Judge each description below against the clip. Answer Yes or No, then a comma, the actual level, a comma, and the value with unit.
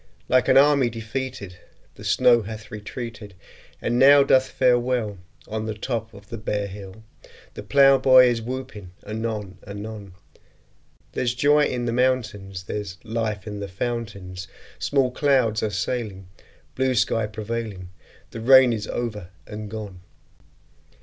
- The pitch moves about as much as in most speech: Yes, average, 3.6 semitones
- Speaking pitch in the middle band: No, low, 110 Hz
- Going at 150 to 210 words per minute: No, average, 140 wpm